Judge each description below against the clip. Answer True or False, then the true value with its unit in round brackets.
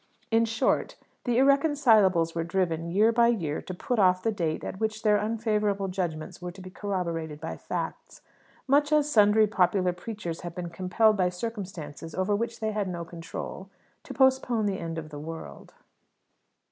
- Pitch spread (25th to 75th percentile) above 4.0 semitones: True (4.6 semitones)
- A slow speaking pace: False (170 wpm)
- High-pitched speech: True (195 Hz)